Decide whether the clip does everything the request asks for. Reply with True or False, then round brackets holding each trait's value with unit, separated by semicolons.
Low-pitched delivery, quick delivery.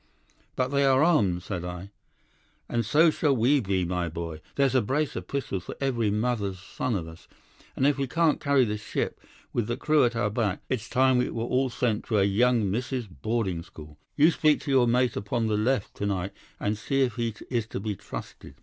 True (115 Hz; 215 wpm)